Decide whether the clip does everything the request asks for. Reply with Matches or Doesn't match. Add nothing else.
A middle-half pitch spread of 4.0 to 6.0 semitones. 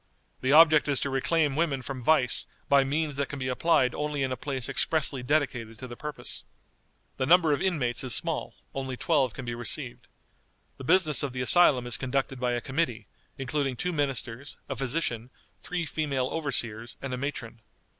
Doesn't match